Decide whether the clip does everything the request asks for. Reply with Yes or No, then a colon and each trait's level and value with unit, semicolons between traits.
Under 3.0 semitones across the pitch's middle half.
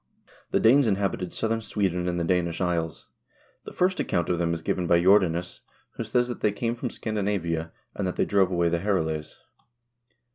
No: average, 3.8 semitones